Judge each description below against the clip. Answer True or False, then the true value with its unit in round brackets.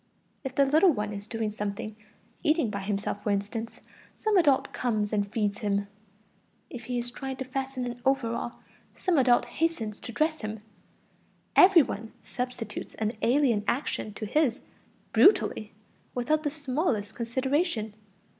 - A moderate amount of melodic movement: True (4.7 semitones)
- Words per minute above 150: False (145 wpm)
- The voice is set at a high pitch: True (240 Hz)